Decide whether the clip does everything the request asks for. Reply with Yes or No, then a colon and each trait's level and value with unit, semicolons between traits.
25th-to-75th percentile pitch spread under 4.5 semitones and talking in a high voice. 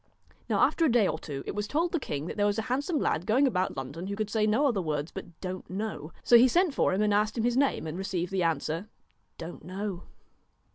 No: average, 5.3 semitones; high, 205 Hz